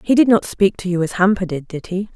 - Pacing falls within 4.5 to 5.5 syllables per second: No, 5.9 syllables/s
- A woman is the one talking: Yes, female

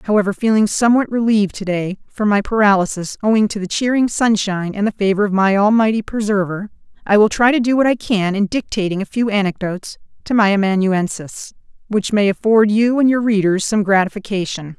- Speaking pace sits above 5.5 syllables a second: Yes, 5.8 syllables/s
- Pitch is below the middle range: No, high, 205 Hz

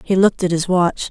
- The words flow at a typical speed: No, fast, 270 wpm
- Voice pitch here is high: No, medium, 180 Hz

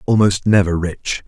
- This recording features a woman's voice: No, male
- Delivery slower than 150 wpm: Yes, average, 140 wpm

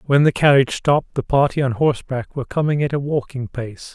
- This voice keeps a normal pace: No, fast, 215 wpm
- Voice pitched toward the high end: No, low, 135 Hz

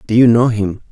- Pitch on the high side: No, low, 115 Hz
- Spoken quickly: Yes, fast, 260 wpm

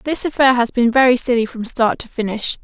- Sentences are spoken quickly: Yes, fast, 230 wpm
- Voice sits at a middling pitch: No, high, 245 Hz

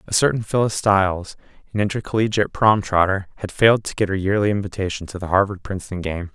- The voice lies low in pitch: Yes, low, 100 Hz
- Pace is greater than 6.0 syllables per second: Yes, 6.5 syllables/s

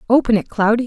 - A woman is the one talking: Yes, female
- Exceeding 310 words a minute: No, fast, 205 wpm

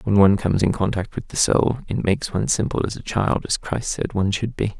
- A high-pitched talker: No, low, 105 Hz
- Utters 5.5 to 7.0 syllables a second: Yes, 6.1 syllables/s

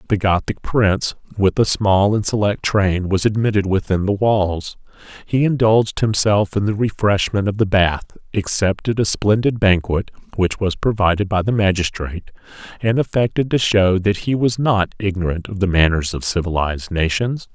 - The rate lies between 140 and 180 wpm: Yes, average, 165 wpm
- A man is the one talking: Yes, male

